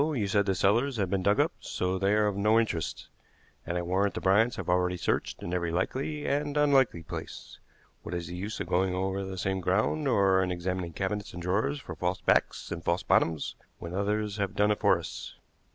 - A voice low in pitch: Yes, very low, 95 Hz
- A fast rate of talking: Yes, fast, 215 wpm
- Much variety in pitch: No, average, 2.9 semitones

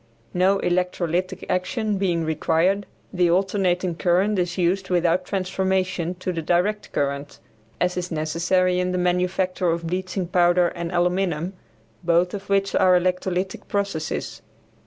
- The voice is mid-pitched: Yes, medium, 180 Hz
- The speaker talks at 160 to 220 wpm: No, slow, 135 wpm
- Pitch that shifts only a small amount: Yes, narrow, 1.5 semitones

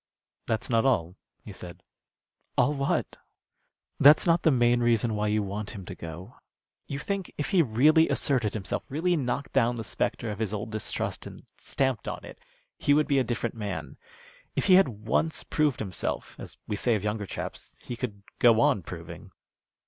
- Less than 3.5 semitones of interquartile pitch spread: No, average, 5.0 semitones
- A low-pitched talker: Yes, low, 120 Hz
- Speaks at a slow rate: No, average, 185 wpm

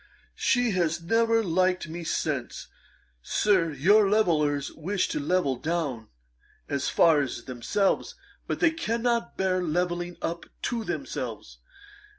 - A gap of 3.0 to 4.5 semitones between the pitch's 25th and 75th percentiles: No, average, 5.3 semitones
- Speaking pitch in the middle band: Yes, medium, 175 Hz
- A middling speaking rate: No, slow, 125 wpm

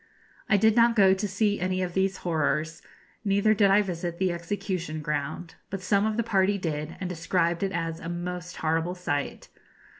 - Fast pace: No, average, 185 wpm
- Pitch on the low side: No, medium, 180 Hz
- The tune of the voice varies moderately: Yes, average, 3.0 semitones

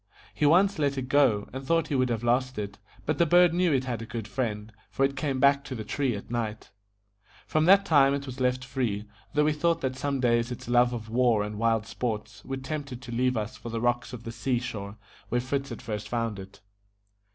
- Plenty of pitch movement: No, average, 3.4 semitones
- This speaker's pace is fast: Yes, fast, 240 wpm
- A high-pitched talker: No, low, 125 Hz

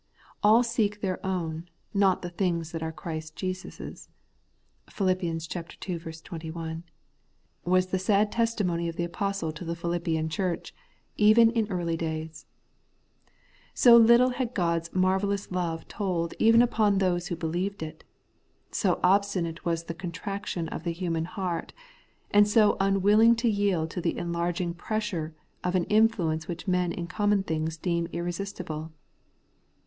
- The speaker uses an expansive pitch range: No, average, 3.3 semitones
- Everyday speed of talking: Yes, average, 145 wpm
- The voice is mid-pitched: Yes, medium, 180 Hz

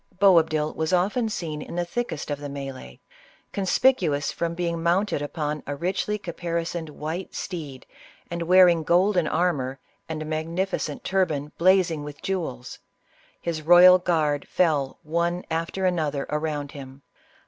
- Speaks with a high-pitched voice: No, medium, 165 Hz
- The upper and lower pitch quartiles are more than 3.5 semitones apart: No, average, 3.2 semitones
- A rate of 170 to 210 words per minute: No, average, 140 wpm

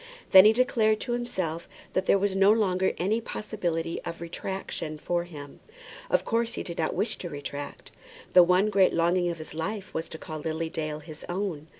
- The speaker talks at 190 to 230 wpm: Yes, average, 195 wpm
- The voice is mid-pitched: Yes, medium, 175 Hz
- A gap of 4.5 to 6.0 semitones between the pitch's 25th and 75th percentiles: No, average, 4.0 semitones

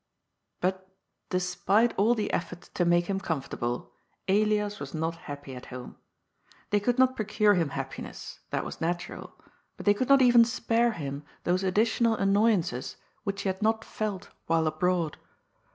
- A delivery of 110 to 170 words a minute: Yes, average, 165 wpm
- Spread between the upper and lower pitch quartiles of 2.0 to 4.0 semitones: No, average, 4.5 semitones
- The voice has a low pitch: No, high, 190 Hz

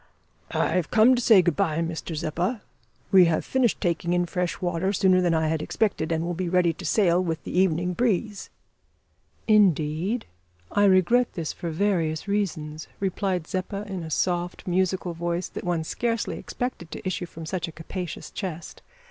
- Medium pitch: Yes, medium, 180 Hz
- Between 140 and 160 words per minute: No, average, 175 wpm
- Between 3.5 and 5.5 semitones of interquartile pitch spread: No, average, 2.9 semitones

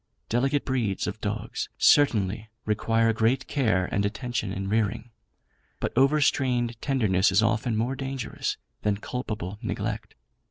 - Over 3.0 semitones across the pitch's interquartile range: Yes, average, 3.4 semitones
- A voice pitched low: Yes, low, 115 Hz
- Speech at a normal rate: No, slow, 125 wpm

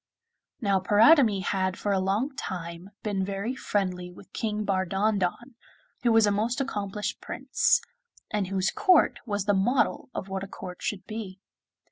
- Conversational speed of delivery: Yes, average, 155 wpm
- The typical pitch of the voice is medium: No, high, 200 Hz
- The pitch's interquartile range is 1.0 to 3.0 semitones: Yes, narrow, 2.4 semitones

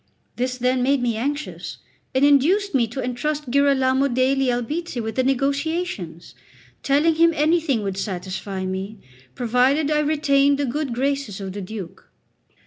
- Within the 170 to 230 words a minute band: No, average, 145 wpm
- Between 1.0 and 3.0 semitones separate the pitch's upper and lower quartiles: No, average, 3.9 semitones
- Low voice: No, very high, 265 Hz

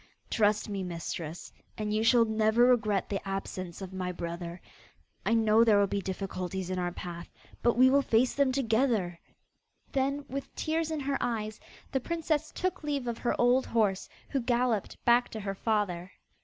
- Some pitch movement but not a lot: Yes, average, 4.9 semitones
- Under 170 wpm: No, average, 175 wpm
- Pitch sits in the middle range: No, high, 220 Hz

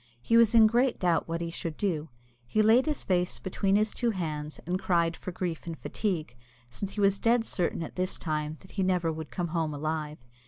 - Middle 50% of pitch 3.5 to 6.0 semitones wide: Yes, average, 4.3 semitones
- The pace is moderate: No, fast, 220 wpm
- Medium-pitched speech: Yes, medium, 180 Hz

